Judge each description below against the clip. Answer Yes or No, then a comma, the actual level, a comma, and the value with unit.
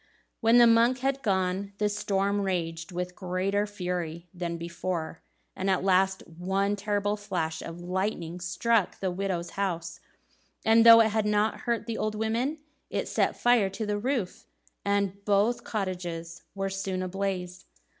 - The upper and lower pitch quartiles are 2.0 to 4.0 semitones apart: Yes, average, 2.8 semitones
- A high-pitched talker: Yes, high, 195 Hz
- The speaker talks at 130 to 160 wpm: Yes, average, 155 wpm